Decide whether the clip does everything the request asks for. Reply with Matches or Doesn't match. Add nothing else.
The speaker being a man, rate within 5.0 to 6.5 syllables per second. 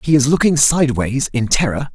Matches